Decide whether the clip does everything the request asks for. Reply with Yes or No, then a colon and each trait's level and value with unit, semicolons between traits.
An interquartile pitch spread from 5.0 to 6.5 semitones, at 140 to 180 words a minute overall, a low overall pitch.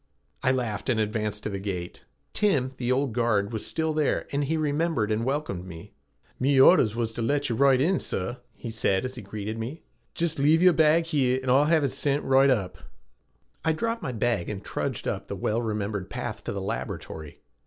No: average, 5.3 semitones; fast, 205 wpm; low, 125 Hz